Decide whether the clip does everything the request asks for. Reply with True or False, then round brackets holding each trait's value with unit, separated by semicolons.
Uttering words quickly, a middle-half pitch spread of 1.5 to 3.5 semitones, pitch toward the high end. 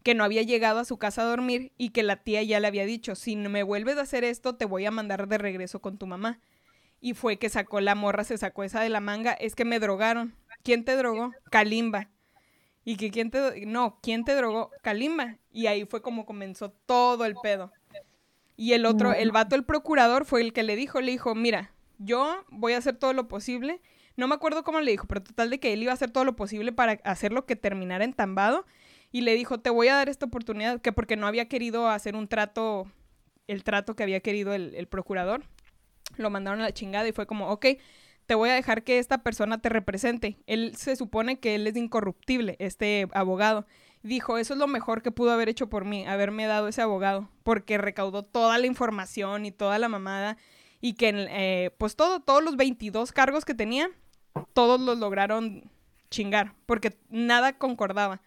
True (215 wpm; 3.0 semitones; 225 Hz)